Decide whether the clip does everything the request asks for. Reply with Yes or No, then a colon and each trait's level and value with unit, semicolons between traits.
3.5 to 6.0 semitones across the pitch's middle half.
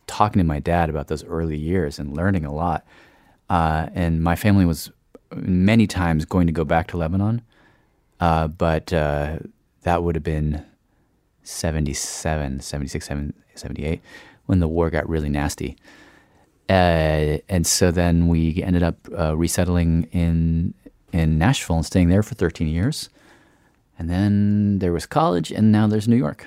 No: narrow, 2.6 semitones